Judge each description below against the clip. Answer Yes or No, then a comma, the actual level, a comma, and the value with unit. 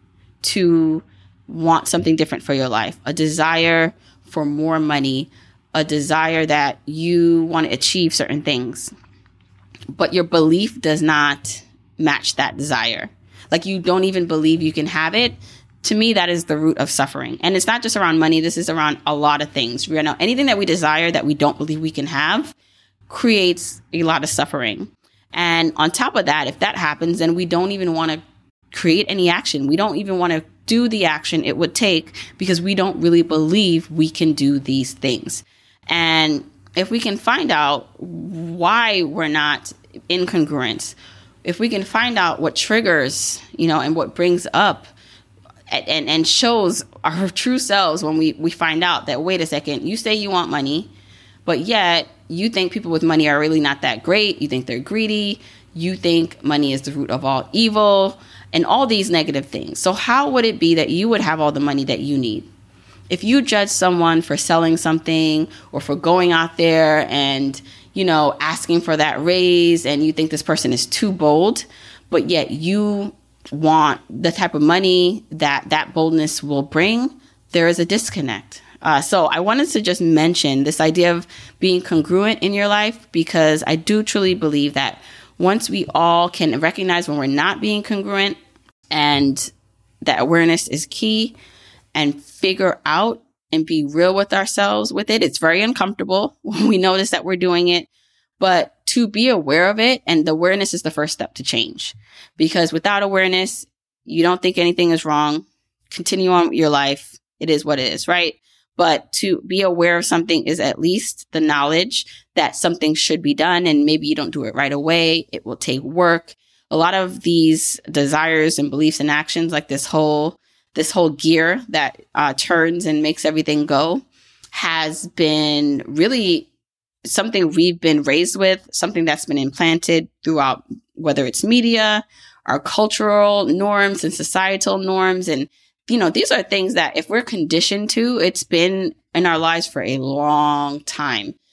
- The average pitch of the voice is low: No, medium, 165 Hz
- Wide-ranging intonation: No, average, 3.7 semitones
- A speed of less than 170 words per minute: No, average, 180 wpm